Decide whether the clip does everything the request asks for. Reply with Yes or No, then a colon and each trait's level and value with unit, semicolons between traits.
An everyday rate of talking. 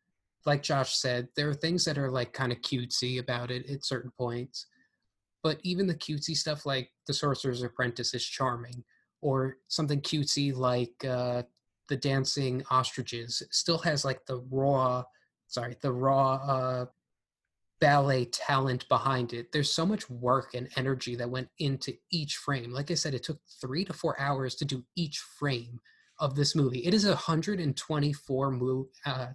Yes: average, 165 wpm